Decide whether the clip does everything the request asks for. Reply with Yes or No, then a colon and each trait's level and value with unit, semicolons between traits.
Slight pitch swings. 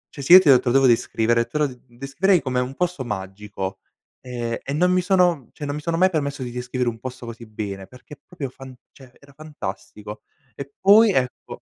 No: average, 4.7 semitones